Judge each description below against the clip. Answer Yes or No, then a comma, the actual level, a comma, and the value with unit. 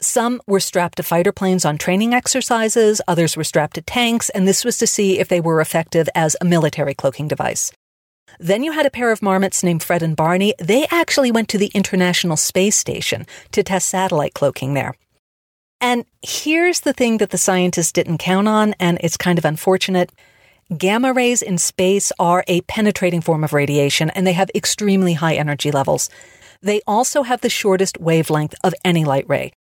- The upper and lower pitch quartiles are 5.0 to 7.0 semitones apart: No, average, 4.3 semitones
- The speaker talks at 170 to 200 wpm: Yes, average, 190 wpm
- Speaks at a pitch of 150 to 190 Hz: Yes, medium, 185 Hz